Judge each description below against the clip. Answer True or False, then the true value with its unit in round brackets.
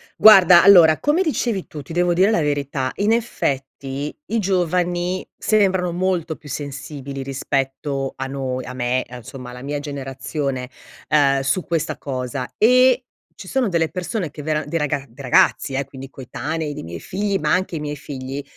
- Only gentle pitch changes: False (5.1 semitones)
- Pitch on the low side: False (150 Hz)